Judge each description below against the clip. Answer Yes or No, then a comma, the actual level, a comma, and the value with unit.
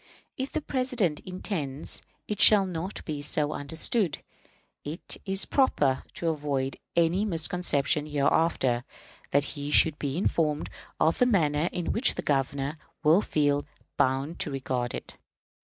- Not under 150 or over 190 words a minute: No, average, 140 wpm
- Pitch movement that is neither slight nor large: Yes, average, 4.1 semitones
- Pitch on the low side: No, medium, 155 Hz